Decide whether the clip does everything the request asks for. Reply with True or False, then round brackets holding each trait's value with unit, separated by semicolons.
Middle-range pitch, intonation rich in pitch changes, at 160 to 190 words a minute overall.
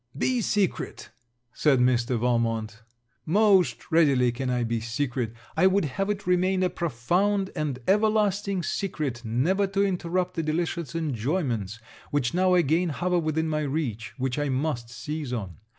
False (155 Hz; 6.9 semitones; 150 wpm)